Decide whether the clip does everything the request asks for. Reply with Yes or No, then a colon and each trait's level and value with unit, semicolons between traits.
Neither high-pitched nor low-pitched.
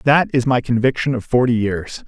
No: low, 120 Hz